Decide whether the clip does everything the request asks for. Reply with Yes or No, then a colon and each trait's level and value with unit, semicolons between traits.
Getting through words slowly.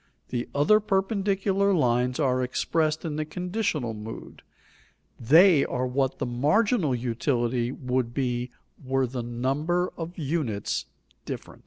Yes: slow, 125 wpm